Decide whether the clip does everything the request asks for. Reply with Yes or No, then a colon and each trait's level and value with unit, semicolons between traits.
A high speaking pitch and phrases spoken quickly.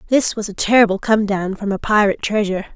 Yes: high, 205 Hz; fast, 220 wpm